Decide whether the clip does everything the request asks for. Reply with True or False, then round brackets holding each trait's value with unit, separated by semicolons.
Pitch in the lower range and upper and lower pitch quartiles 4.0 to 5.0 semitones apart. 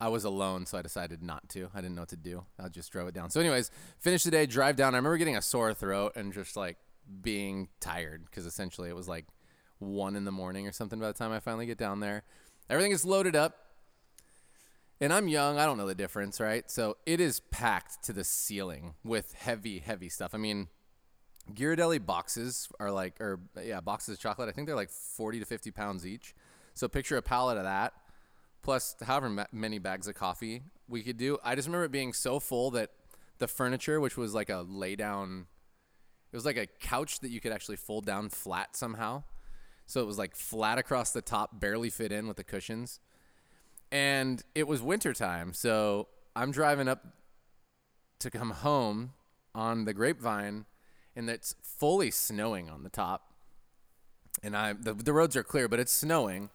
True (110 Hz; 4.7 semitones)